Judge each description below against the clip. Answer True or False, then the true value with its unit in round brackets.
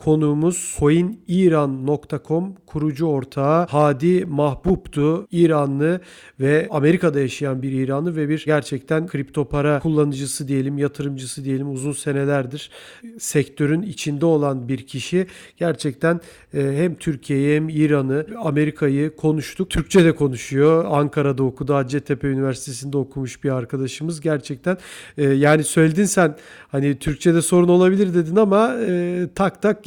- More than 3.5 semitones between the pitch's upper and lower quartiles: False (3.2 semitones)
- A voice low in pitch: False (150 Hz)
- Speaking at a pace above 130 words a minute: False (115 wpm)